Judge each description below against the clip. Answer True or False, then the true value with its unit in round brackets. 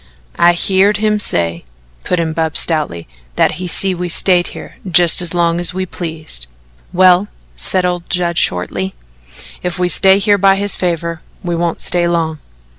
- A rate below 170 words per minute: False (175 wpm)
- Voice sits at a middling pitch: True (175 Hz)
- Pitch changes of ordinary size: False (2.1 semitones)